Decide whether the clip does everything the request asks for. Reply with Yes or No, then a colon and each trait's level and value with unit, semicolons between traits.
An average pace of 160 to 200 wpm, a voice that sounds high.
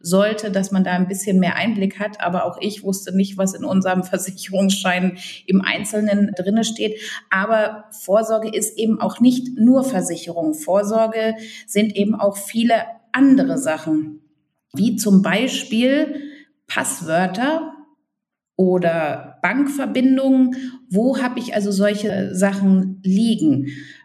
No: slow, 125 wpm; high, 205 Hz